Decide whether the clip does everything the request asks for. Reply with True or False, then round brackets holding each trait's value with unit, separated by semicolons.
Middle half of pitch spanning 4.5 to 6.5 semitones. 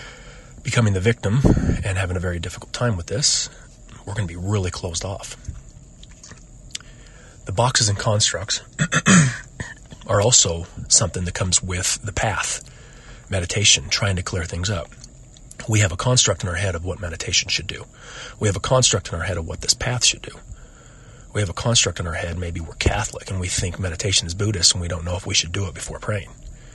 True (4.9 semitones)